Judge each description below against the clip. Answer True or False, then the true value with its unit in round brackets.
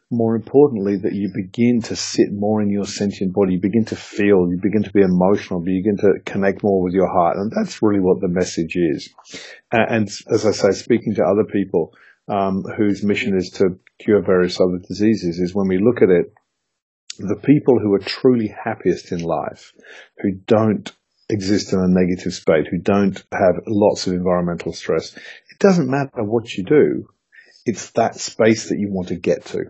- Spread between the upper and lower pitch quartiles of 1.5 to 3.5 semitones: True (2.9 semitones)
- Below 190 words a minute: False (195 wpm)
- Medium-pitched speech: False (100 Hz)